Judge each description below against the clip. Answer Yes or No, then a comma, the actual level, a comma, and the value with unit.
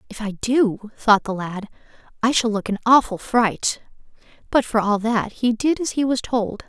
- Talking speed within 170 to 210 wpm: Yes, average, 200 wpm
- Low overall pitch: No, high, 225 Hz